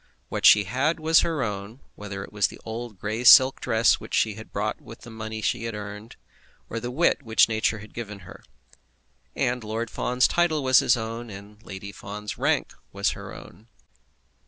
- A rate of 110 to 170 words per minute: No, average, 185 wpm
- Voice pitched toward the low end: Yes, low, 110 Hz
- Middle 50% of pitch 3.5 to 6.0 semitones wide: No, average, 2.7 semitones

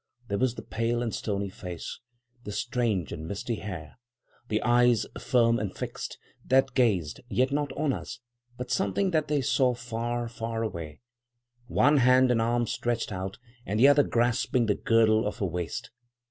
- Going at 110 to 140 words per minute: No, average, 170 wpm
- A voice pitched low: Yes, low, 115 Hz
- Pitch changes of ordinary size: Yes, average, 3.3 semitones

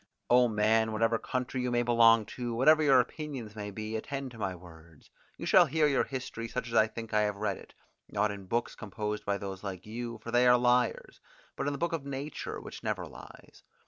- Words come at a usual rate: No, fast, 220 wpm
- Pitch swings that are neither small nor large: Yes, average, 3.1 semitones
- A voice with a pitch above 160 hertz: No, low, 115 Hz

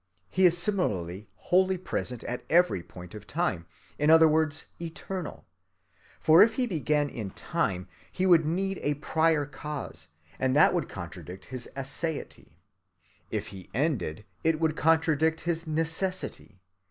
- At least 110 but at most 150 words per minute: Yes, average, 140 wpm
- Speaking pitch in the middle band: Yes, medium, 155 Hz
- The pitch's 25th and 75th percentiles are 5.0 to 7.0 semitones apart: Yes, average, 5.3 semitones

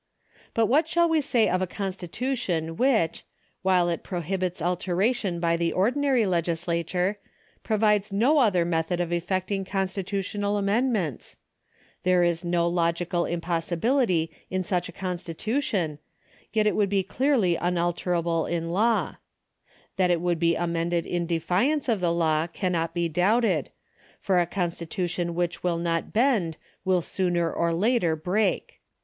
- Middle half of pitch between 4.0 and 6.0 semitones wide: No, average, 3.3 semitones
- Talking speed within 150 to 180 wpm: No, average, 140 wpm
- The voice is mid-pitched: Yes, medium, 180 Hz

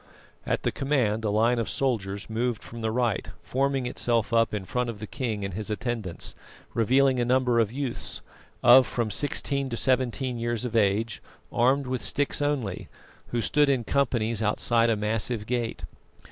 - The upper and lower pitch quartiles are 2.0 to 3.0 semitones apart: Yes, average, 2.7 semitones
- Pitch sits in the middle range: No, low, 120 Hz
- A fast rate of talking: No, average, 175 wpm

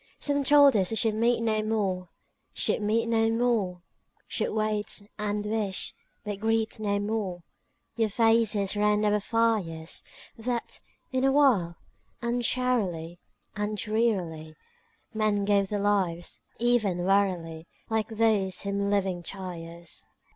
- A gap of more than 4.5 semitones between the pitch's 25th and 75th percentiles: No, average, 3.0 semitones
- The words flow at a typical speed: No, slow, 125 wpm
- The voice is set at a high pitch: Yes, high, 210 Hz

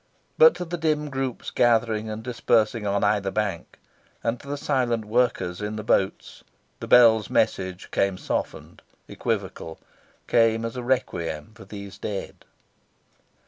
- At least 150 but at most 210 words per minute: No, average, 140 wpm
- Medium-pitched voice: No, low, 110 Hz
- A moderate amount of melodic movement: Yes, average, 3.6 semitones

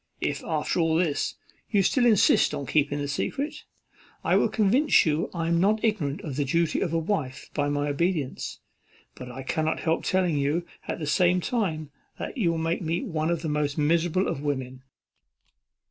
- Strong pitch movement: No, average, 3.9 semitones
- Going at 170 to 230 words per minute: Yes, average, 185 wpm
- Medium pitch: Yes, medium, 160 Hz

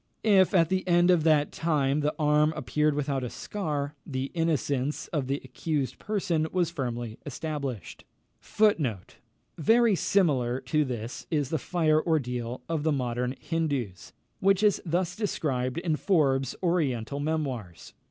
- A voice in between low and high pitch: Yes, medium, 150 Hz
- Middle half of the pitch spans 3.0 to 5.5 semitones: Yes, average, 4.3 semitones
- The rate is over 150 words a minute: No, average, 140 wpm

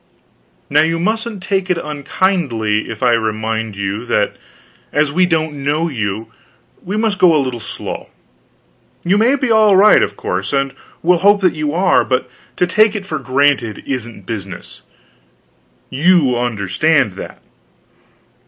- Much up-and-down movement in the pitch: Yes, wide, 8.2 semitones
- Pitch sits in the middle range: Yes, medium, 150 Hz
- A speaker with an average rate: Yes, average, 150 wpm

